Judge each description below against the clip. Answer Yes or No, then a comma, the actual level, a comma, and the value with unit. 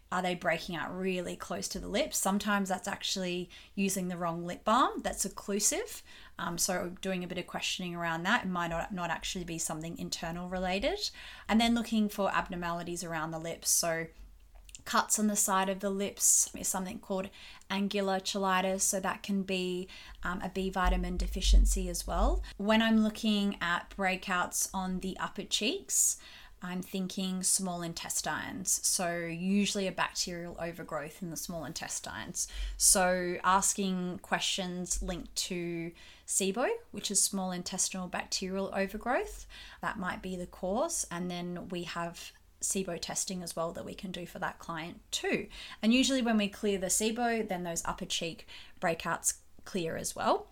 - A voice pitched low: No, medium, 185 Hz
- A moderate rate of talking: Yes, average, 165 wpm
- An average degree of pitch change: No, narrow, 2.3 semitones